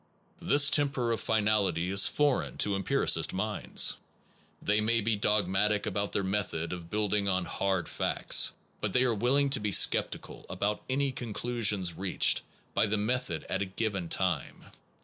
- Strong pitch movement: No, average, 3.3 semitones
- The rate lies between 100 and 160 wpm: Yes, average, 155 wpm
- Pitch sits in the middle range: No, low, 105 Hz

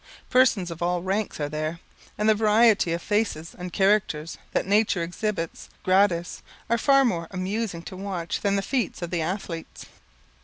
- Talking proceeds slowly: No, average, 165 wpm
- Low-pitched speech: No, medium, 185 Hz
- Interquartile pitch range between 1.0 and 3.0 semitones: No, average, 3.9 semitones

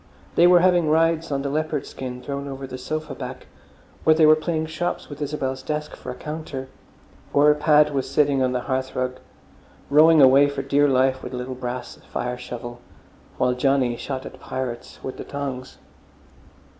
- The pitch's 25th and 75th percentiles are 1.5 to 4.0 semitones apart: Yes, average, 2.9 semitones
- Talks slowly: No, average, 180 wpm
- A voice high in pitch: No, medium, 140 Hz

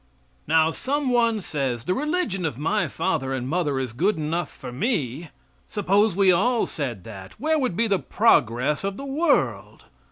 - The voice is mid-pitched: Yes, medium, 180 Hz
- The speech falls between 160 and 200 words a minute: Yes, average, 170 wpm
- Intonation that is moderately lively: No, wide, 8.8 semitones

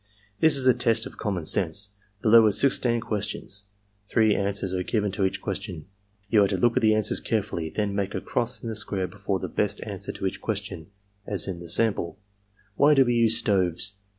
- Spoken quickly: Yes, fast, 220 wpm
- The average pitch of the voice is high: No, low, 105 Hz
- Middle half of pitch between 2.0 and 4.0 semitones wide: Yes, average, 2.9 semitones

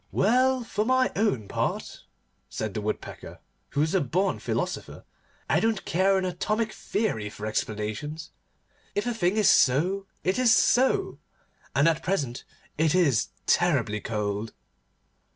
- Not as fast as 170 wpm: Yes, average, 140 wpm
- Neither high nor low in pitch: Yes, medium, 175 Hz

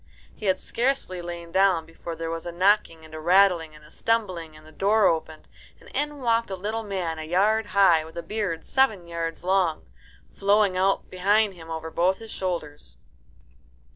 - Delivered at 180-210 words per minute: Yes, average, 185 wpm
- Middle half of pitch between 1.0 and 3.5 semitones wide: No, average, 3.9 semitones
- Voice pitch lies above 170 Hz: Yes, medium, 185 Hz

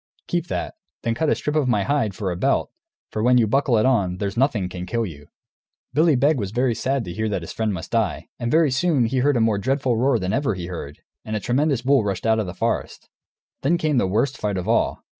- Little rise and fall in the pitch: No, average, 5.3 semitones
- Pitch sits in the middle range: No, low, 115 Hz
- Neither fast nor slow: No, fast, 255 wpm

